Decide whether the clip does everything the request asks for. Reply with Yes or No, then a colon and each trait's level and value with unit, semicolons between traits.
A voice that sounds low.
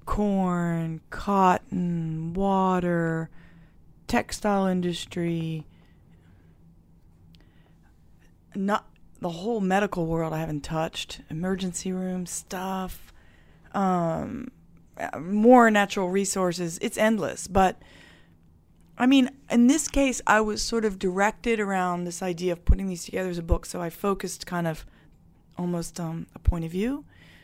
No: medium, 180 Hz